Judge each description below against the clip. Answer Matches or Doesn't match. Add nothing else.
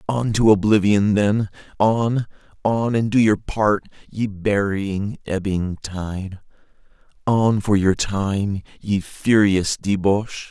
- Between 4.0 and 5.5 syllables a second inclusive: Doesn't match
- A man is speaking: Matches